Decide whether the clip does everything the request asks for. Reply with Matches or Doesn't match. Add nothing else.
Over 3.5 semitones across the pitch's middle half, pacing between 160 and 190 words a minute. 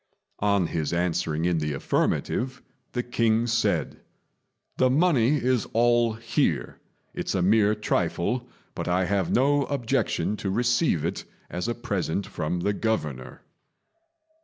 Doesn't match